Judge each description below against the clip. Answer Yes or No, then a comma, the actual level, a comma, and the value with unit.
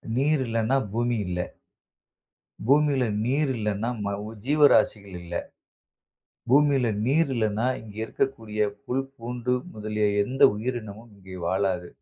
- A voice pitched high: No, low, 115 Hz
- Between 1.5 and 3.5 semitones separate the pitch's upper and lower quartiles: No, average, 4.0 semitones